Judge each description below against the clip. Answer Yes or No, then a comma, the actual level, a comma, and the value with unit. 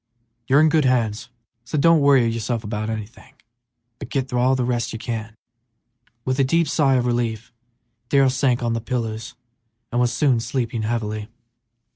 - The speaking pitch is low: Yes, low, 120 Hz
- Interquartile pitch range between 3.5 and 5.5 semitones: No, average, 2.7 semitones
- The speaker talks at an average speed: Yes, average, 165 wpm